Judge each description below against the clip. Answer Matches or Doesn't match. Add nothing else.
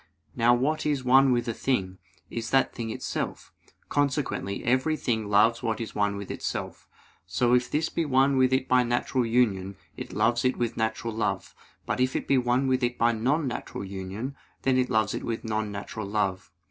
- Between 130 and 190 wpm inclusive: Doesn't match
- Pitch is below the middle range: Matches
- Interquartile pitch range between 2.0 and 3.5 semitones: Matches